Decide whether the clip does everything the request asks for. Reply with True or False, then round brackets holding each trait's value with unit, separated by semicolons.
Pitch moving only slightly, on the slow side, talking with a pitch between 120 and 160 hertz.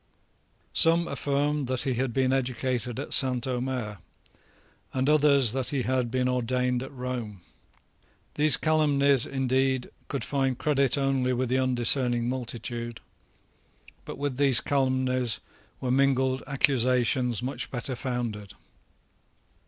True (1.8 semitones; 120 wpm; 130 Hz)